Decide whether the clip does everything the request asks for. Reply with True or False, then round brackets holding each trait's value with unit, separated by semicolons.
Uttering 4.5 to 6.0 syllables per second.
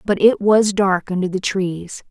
False (4.1 syllables/s)